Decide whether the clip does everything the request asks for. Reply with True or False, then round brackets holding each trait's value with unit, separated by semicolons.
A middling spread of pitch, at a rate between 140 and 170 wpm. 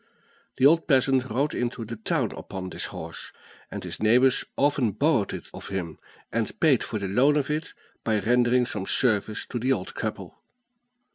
False (3.9 semitones; 180 wpm)